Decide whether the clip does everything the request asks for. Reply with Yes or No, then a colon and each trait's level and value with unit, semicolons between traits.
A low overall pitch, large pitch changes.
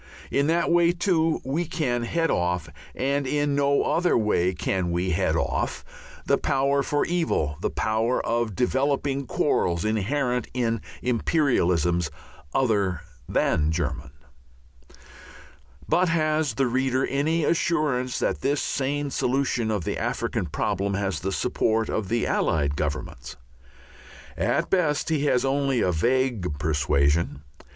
Yes: low, 125 Hz; wide, 7.7 semitones